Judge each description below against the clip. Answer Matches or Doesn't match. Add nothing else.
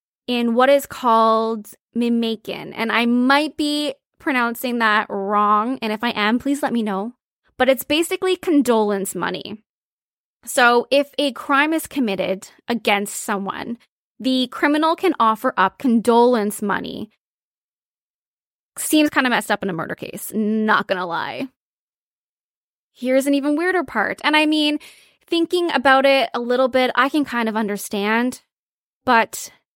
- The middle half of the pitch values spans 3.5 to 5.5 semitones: Matches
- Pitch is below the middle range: Doesn't match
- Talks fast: Doesn't match